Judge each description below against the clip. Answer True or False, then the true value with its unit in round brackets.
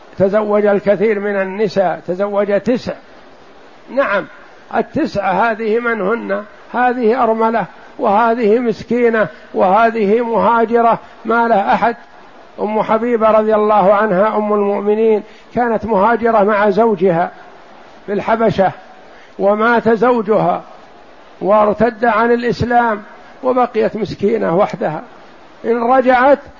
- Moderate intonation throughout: False (2.1 semitones)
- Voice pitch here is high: True (220 Hz)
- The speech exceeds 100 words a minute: False (95 wpm)